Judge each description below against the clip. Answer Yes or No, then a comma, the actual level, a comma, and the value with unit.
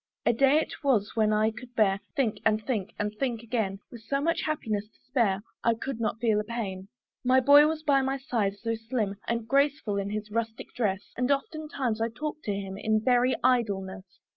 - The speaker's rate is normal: No, fast, 210 wpm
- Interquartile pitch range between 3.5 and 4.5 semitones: Yes, average, 3.9 semitones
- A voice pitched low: No, high, 230 Hz